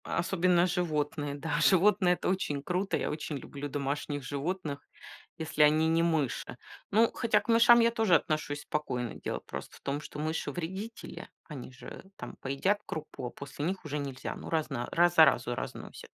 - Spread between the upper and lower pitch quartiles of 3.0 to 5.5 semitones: Yes, average, 4.0 semitones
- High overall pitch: No, medium, 155 Hz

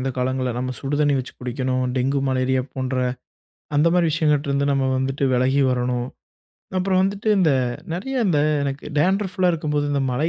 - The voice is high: No, medium, 140 Hz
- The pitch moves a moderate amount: Yes, average, 4.2 semitones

